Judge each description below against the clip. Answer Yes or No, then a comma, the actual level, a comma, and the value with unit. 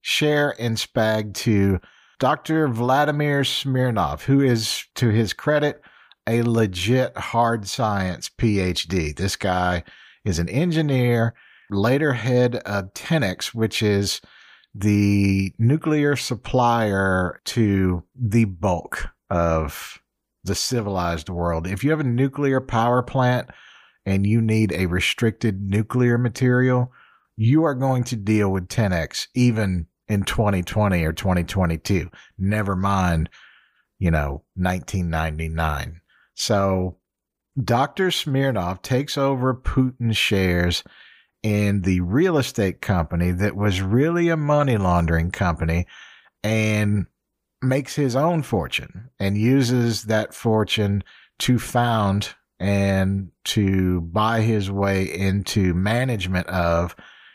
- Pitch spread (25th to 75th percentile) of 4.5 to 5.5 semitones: Yes, average, 5.0 semitones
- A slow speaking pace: Yes, slow, 110 wpm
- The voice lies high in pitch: No, low, 105 Hz